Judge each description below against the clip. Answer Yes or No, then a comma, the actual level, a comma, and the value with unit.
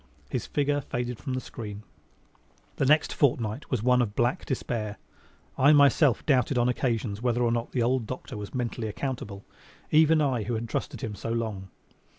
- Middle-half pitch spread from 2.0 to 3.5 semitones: Yes, average, 3.1 semitones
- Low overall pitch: Yes, low, 120 Hz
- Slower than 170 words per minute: No, average, 175 wpm